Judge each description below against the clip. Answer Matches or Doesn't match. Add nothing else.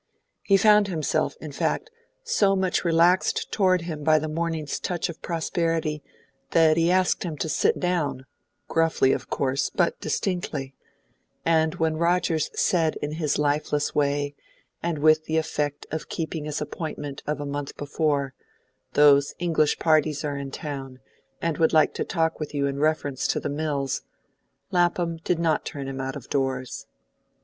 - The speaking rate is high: Doesn't match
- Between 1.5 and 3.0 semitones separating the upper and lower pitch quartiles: Matches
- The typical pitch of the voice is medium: Matches